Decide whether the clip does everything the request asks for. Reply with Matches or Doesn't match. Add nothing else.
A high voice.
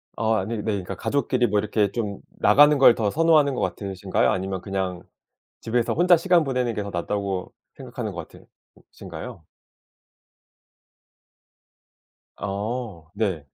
Doesn't match